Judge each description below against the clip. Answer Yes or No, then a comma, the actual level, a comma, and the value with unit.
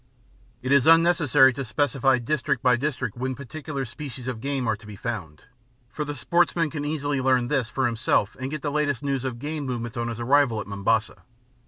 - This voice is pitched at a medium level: No, low, 130 Hz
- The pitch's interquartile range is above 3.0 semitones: Yes, average, 3.5 semitones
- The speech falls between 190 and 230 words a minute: Yes, average, 200 wpm